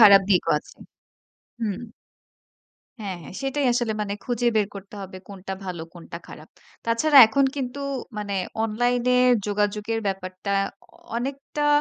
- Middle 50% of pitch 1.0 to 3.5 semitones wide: No, average, 3.9 semitones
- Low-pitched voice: No, high, 210 Hz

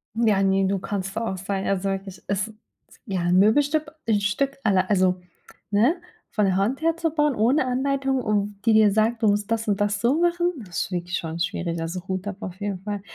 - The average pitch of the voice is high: Yes, high, 205 Hz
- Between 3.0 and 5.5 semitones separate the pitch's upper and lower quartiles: Yes, average, 3.7 semitones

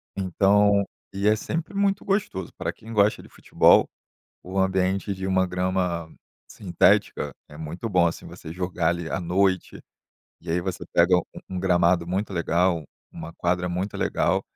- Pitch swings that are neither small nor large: No, narrow, 2.1 semitones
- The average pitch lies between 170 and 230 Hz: No, very low, 95 Hz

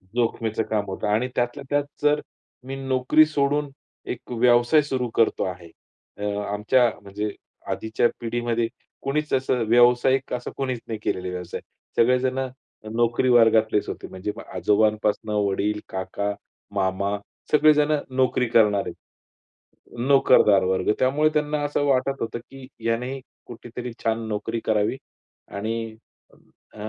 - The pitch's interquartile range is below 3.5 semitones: No, average, 3.9 semitones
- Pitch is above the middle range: No, low, 120 Hz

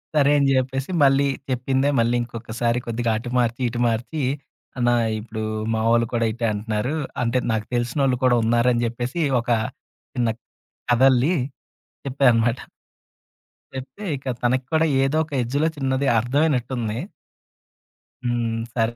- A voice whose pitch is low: Yes, low, 120 Hz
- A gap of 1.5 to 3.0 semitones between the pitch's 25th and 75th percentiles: Yes, narrow, 2.4 semitones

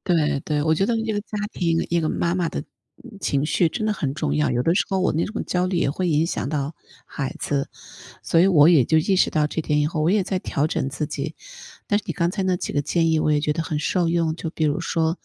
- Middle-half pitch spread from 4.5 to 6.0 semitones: No, average, 3.3 semitones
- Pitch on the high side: No, medium, 165 Hz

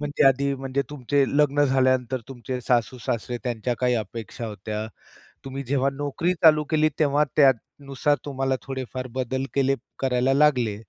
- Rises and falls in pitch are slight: Yes, narrow, 2.3 semitones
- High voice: No, low, 135 Hz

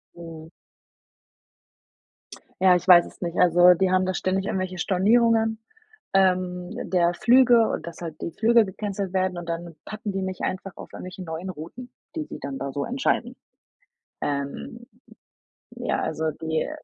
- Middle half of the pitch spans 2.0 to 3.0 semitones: No, average, 3.4 semitones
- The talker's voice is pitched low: No, medium, 185 Hz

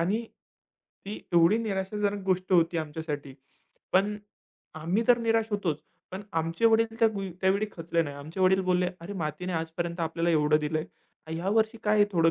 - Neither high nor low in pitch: Yes, medium, 180 Hz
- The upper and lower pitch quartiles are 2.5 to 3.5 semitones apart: No, average, 4.0 semitones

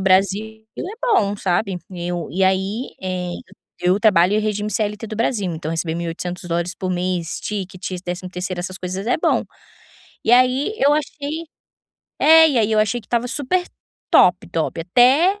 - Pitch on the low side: No, high, 195 Hz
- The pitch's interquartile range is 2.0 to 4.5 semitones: No, average, 4.9 semitones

